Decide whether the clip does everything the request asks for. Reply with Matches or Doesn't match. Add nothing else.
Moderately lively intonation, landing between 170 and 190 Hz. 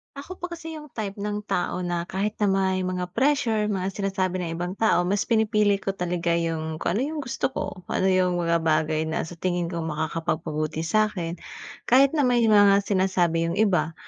Matches